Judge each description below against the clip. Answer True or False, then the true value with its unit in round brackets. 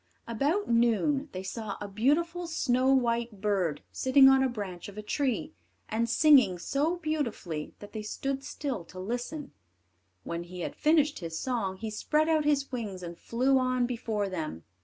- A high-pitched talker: True (240 Hz)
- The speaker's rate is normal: True (170 wpm)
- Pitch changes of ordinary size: False (5.7 semitones)